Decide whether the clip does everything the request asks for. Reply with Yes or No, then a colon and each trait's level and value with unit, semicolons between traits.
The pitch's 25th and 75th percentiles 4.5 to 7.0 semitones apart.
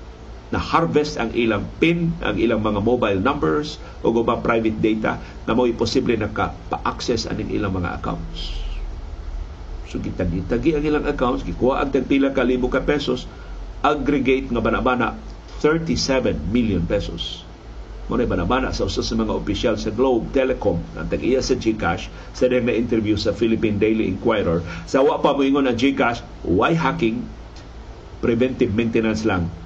Yes: wide, 5.6 semitones